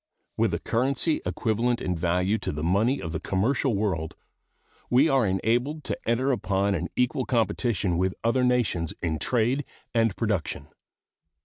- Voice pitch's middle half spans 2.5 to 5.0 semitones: No, wide, 5.4 semitones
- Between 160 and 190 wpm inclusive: No, average, 150 wpm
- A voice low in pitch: Yes, low, 110 Hz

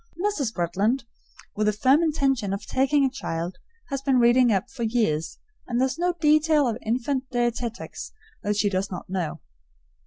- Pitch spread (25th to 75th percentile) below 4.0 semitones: No, average, 4.8 semitones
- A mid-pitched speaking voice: No, high, 240 Hz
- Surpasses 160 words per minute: Yes, average, 175 wpm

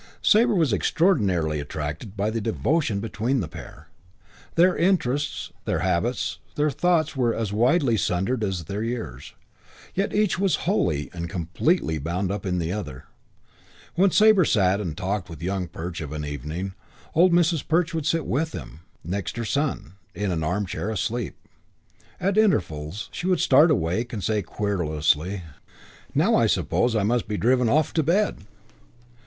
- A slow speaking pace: No, average, 160 wpm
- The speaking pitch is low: Yes, low, 110 Hz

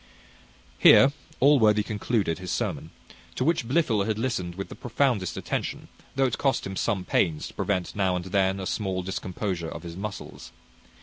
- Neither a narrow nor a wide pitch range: Yes, average, 4.1 semitones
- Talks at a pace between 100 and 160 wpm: No, average, 170 wpm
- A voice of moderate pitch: No, low, 100 Hz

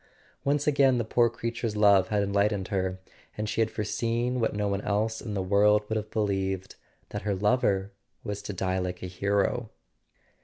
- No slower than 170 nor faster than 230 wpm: Yes, average, 185 wpm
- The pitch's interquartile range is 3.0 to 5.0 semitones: No, narrow, 2.4 semitones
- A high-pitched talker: No, low, 105 Hz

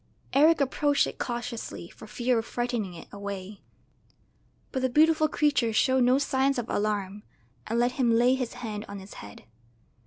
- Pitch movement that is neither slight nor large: Yes, average, 3.9 semitones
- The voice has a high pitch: Yes, high, 240 Hz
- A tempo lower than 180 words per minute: Yes, average, 165 wpm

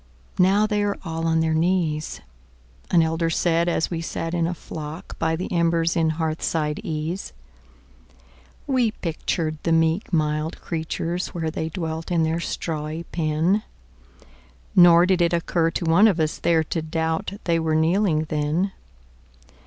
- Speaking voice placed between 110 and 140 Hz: No, medium, 160 Hz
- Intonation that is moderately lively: No, narrow, 1.8 semitones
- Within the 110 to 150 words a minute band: Yes, average, 145 wpm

